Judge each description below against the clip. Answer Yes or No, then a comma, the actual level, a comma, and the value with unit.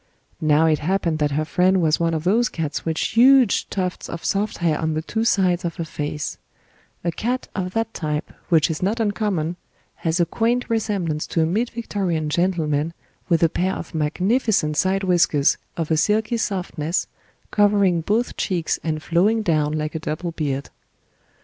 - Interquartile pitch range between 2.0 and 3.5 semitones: No, average, 4.5 semitones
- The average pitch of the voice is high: No, medium, 175 Hz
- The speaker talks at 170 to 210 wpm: Yes, average, 175 wpm